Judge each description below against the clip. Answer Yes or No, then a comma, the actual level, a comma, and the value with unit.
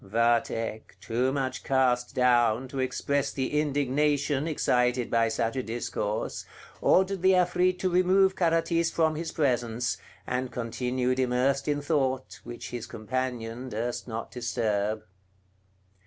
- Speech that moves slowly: Yes, slow, 125 wpm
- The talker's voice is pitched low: Yes, low, 130 Hz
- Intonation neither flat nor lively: Yes, average, 3.9 semitones